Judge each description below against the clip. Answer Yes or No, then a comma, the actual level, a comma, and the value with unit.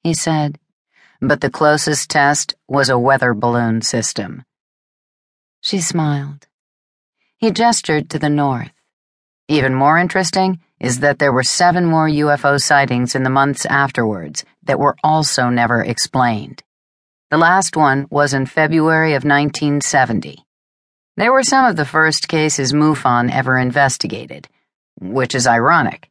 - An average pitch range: Yes, average, 4.1 semitones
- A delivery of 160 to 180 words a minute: No, slow, 135 wpm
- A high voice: No, medium, 140 Hz